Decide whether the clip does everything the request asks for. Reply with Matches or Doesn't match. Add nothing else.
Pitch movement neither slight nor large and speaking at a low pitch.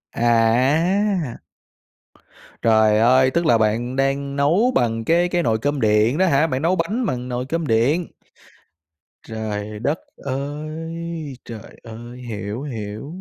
Doesn't match